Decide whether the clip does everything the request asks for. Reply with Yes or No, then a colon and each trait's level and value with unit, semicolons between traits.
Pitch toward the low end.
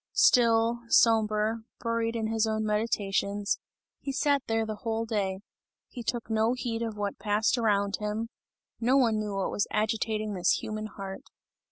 No: high, 220 Hz